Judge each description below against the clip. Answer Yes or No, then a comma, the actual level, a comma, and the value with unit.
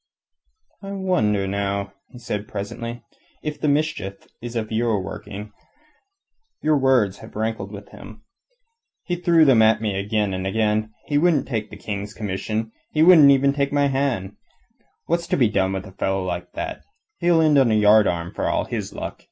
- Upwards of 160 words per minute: Yes, average, 175 wpm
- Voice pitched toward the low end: Yes, low, 110 Hz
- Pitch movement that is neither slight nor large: No, wide, 5.8 semitones